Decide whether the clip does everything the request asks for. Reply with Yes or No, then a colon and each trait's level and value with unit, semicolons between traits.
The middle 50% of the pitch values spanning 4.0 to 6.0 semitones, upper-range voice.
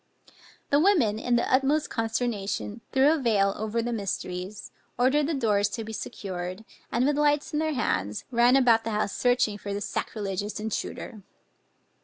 Yes: average, 4.4 semitones; high, 225 Hz